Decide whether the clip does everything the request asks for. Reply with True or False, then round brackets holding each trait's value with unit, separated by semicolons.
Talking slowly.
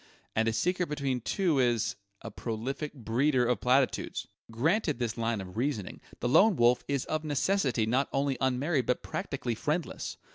False (160 wpm)